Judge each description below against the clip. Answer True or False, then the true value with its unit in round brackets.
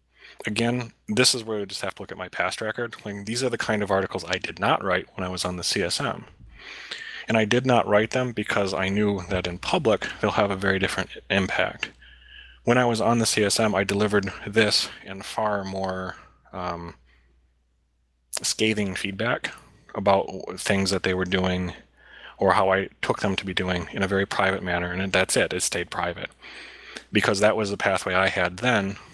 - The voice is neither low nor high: False (95 Hz)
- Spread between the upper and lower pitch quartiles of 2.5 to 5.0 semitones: True (2.8 semitones)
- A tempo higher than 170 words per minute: True (200 wpm)